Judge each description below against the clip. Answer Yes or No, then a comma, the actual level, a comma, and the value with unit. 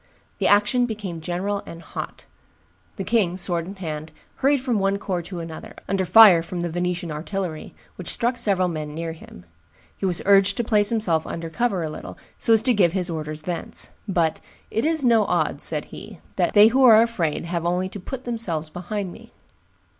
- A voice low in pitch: No, medium, 185 Hz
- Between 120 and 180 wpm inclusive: No, average, 190 wpm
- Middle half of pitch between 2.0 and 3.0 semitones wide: No, average, 4.5 semitones